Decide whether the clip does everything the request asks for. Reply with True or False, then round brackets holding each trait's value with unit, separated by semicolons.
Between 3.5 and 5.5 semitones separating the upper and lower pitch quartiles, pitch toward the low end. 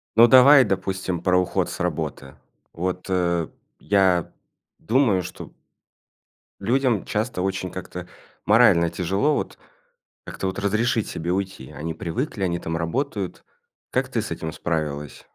True (3.8 semitones; 95 Hz)